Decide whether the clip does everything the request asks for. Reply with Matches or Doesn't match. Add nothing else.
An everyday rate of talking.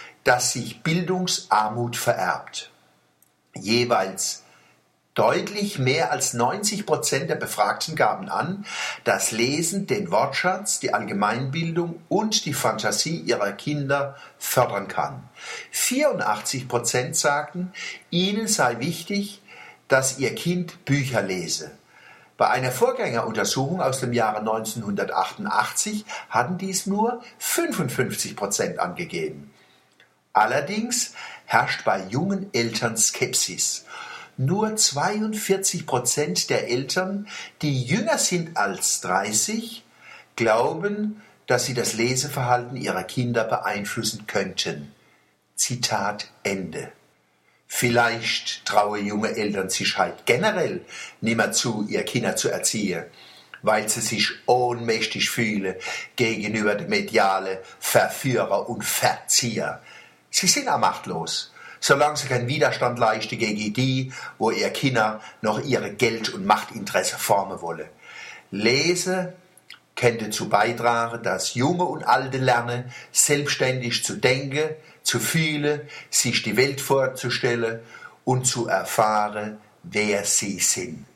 Doesn't match